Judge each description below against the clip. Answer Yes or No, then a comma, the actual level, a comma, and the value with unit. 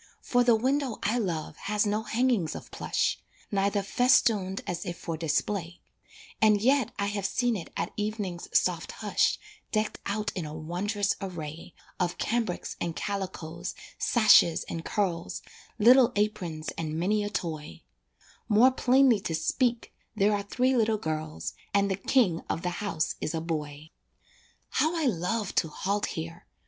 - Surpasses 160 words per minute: No, average, 155 wpm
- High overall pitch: Yes, high, 200 Hz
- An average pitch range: Yes, average, 4.7 semitones